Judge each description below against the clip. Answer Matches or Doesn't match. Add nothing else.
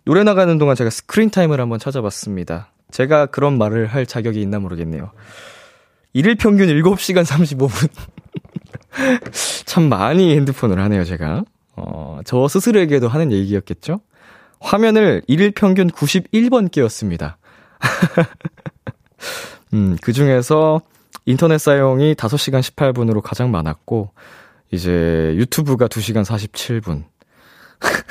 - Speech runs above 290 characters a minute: Doesn't match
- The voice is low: Matches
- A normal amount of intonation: Doesn't match